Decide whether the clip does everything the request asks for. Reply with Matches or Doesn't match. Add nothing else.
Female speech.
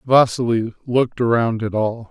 Doesn't match